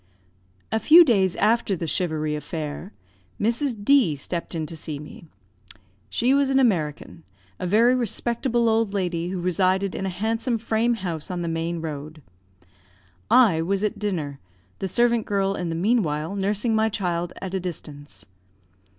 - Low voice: No, high, 190 Hz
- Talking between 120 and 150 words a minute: No, average, 160 wpm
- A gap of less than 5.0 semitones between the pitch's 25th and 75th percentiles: No, wide, 5.4 semitones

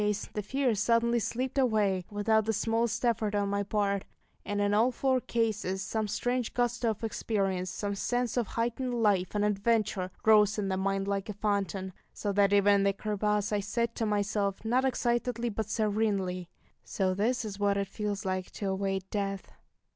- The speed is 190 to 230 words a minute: Yes, average, 195 wpm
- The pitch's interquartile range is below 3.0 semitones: Yes, narrow, 2.5 semitones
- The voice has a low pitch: No, high, 210 Hz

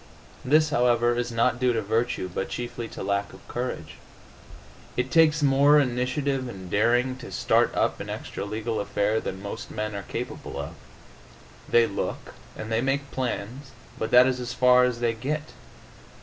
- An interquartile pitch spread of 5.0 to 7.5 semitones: No, average, 3.0 semitones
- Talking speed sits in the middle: Yes, average, 170 wpm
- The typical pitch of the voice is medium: No, low, 120 Hz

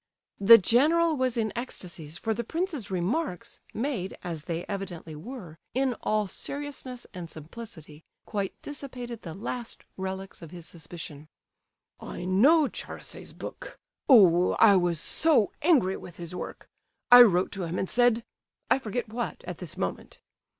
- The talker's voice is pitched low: No, high, 205 Hz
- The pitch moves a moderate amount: No, wide, 6.1 semitones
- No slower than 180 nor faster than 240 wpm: No, average, 145 wpm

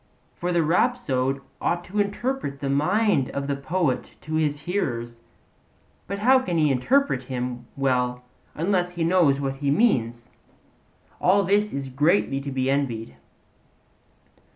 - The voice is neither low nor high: Yes, medium, 145 Hz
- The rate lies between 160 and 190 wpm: No, average, 140 wpm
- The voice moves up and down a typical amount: No, wide, 5.8 semitones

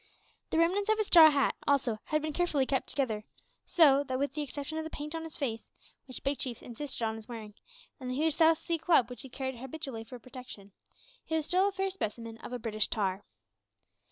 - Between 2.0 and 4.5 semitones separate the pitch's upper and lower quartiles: No, average, 5.1 semitones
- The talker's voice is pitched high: Yes, very high, 275 Hz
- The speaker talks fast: Yes, fast, 220 wpm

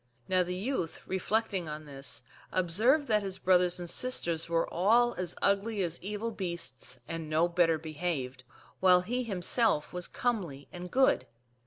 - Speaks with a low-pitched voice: No, medium, 180 Hz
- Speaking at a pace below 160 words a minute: Yes, average, 150 wpm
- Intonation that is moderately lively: Yes, average, 4.2 semitones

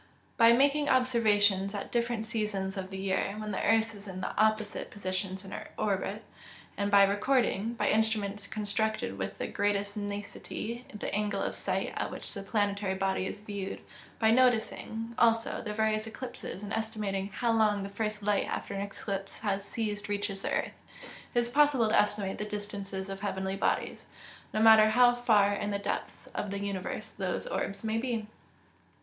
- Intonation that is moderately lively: No, narrow, 2.0 semitones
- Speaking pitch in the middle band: No, high, 210 Hz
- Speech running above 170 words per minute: Yes, average, 180 wpm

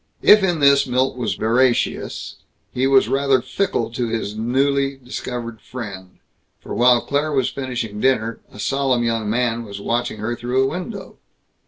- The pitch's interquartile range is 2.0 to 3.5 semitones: Yes, average, 2.9 semitones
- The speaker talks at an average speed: Yes, average, 160 wpm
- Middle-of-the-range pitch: No, low, 125 Hz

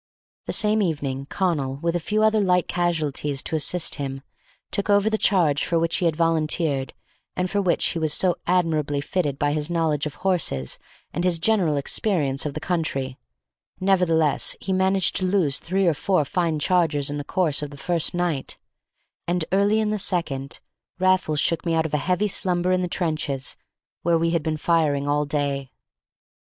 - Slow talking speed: No, average, 185 wpm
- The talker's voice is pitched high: No, medium, 165 Hz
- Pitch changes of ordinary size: Yes, average, 3.9 semitones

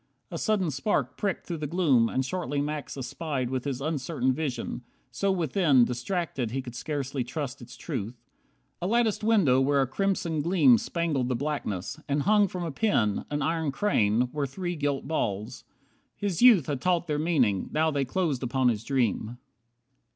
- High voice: No, medium, 145 Hz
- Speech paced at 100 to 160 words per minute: No, average, 175 wpm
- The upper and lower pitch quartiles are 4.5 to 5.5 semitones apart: Yes, average, 5.1 semitones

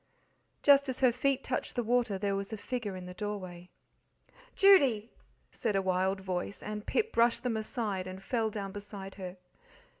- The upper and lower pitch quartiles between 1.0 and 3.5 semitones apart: No, average, 4.1 semitones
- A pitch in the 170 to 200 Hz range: No, high, 210 Hz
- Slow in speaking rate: No, average, 175 wpm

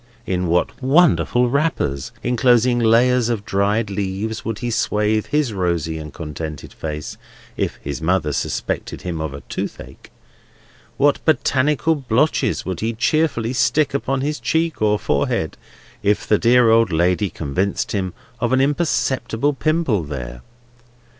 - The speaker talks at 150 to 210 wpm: No, average, 140 wpm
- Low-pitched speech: Yes, low, 110 Hz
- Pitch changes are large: Yes, wide, 6.3 semitones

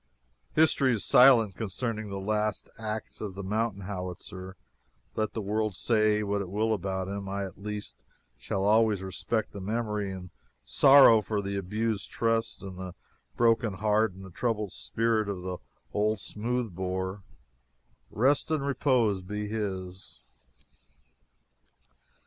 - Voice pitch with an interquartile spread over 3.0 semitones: No, narrow, 2.6 semitones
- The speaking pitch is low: Yes, low, 105 Hz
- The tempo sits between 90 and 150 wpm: Yes, average, 140 wpm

